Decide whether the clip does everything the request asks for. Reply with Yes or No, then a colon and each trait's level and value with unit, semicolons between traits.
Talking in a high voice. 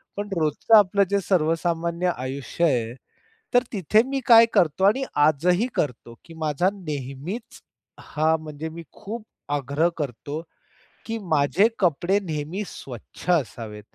No: medium, 165 Hz